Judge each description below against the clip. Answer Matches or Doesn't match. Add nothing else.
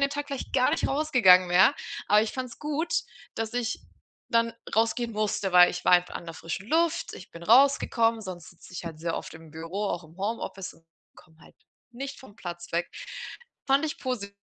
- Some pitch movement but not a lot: Doesn't match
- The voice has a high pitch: Matches